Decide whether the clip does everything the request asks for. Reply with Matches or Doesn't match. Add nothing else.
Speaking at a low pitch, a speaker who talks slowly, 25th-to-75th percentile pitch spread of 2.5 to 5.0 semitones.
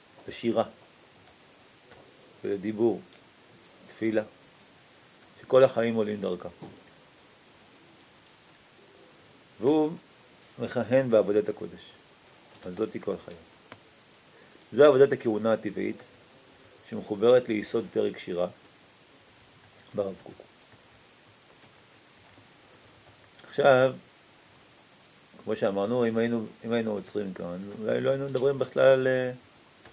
Matches